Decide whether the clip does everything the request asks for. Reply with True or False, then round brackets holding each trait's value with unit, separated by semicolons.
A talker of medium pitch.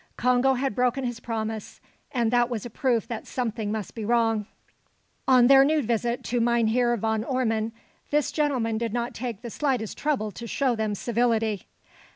False (235 Hz)